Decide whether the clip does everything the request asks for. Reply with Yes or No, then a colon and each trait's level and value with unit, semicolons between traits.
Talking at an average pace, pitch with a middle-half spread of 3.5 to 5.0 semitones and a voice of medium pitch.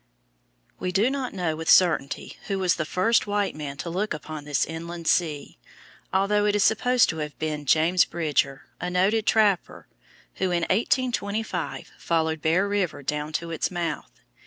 Yes: average, 165 wpm; average, 4.4 semitones; medium, 175 Hz